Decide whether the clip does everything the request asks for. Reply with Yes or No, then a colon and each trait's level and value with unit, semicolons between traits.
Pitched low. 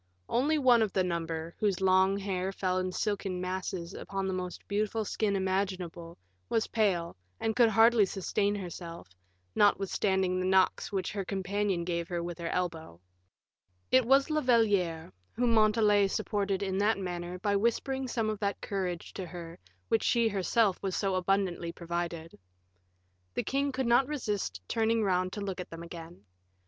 No: high, 195 Hz